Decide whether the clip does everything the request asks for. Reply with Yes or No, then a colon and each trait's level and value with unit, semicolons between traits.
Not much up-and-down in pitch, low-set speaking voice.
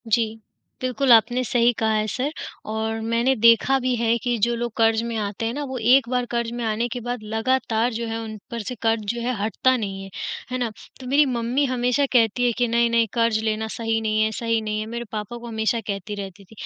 No: narrow, 1.8 semitones; high, 230 Hz